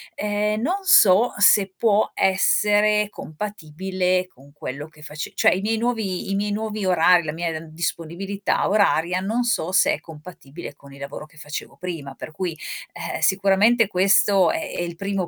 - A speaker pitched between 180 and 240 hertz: Yes, medium, 185 Hz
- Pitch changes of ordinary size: Yes, average, 4.3 semitones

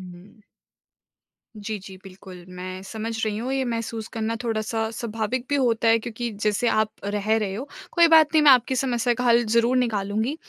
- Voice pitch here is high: Yes, high, 225 Hz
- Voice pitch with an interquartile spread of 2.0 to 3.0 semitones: Yes, narrow, 2.4 semitones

